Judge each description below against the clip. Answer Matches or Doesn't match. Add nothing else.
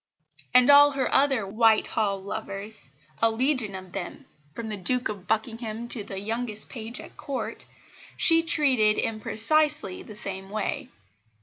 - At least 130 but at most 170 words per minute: Matches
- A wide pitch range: Doesn't match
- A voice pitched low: Doesn't match